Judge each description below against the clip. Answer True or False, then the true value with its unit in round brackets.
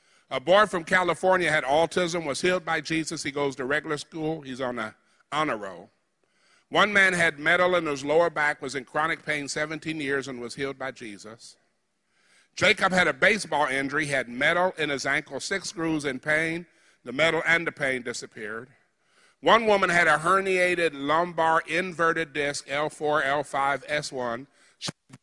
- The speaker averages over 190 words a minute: False (170 wpm)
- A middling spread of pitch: True (3.4 semitones)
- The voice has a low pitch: False (155 Hz)